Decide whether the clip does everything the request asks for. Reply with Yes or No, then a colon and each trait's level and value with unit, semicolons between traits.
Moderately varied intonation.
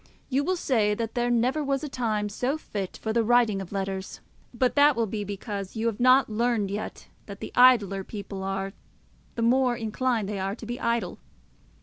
Yes: average, 3.6 semitones